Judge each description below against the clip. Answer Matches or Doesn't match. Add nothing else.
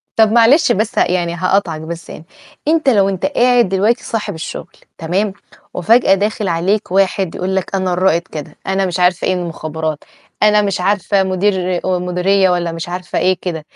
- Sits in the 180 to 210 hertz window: Matches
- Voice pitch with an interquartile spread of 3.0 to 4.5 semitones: Doesn't match